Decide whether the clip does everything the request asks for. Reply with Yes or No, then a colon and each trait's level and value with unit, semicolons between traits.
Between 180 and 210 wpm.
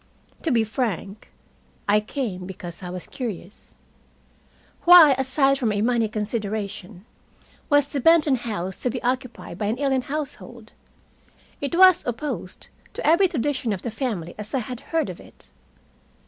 No: average, 150 wpm